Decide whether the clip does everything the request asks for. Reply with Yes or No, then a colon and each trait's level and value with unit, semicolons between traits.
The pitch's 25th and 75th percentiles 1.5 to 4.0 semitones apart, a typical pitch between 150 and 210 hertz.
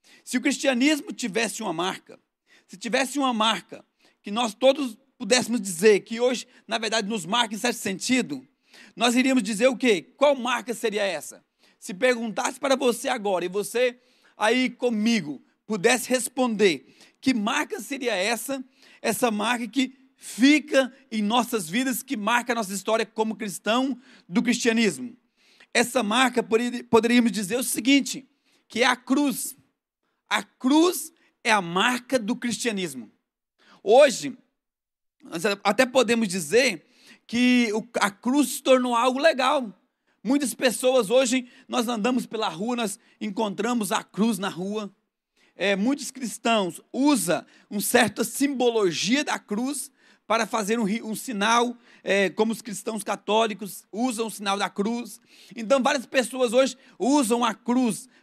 No: average, 2.9 semitones; high, 240 Hz